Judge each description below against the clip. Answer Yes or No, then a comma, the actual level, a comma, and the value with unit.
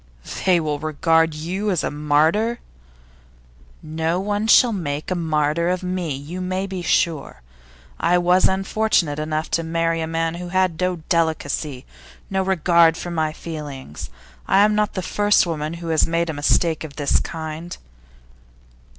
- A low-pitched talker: No, medium, 165 Hz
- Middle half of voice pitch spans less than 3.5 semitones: Yes, average, 2.9 semitones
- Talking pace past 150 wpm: Yes, average, 160 wpm